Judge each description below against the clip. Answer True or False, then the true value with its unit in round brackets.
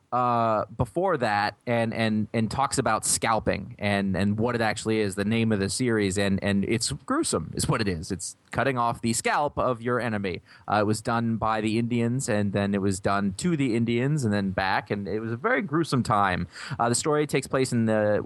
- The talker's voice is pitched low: True (115 Hz)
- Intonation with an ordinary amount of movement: True (3.0 semitones)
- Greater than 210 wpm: True (225 wpm)